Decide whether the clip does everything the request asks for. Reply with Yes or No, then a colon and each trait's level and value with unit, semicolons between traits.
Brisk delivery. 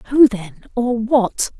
No: average, 150 wpm